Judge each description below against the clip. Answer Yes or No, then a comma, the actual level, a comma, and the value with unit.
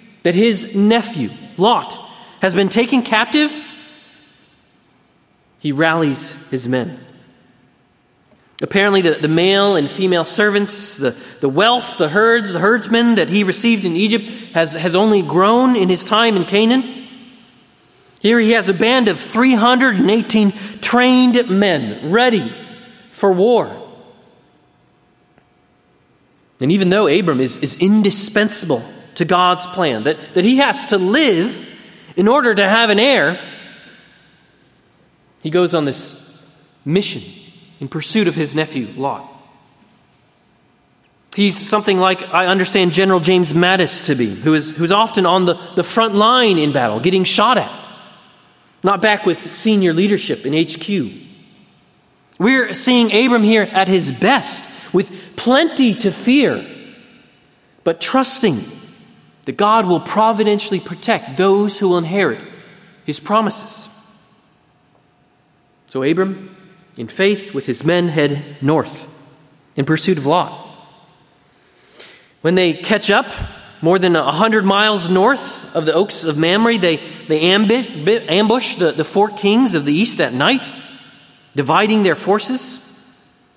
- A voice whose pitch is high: Yes, high, 195 Hz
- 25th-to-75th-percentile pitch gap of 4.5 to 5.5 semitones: Yes, average, 4.9 semitones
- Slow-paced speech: Yes, slow, 130 wpm